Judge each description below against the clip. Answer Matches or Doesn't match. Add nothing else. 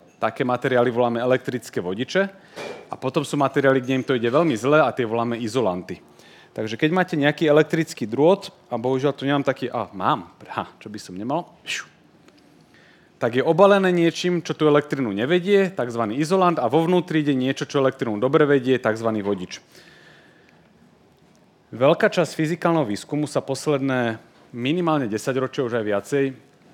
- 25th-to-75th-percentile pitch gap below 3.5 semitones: Doesn't match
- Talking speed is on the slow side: Doesn't match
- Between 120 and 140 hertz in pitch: Matches